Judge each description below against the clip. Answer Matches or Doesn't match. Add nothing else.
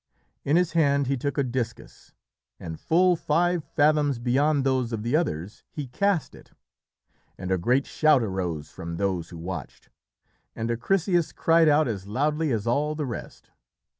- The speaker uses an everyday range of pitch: Doesn't match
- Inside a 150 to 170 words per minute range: Matches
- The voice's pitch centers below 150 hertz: Matches